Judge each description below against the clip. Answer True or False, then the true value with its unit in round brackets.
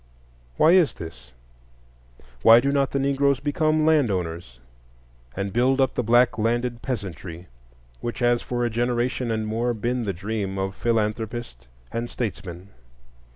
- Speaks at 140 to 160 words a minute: True (145 wpm)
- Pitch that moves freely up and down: False (4.3 semitones)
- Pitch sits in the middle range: False (120 Hz)